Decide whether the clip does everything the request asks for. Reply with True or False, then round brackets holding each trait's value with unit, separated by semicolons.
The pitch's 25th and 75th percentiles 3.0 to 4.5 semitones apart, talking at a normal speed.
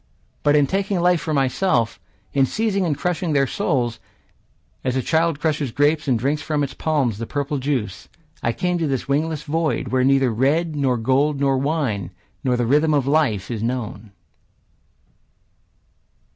True (3.8 semitones; 165 wpm)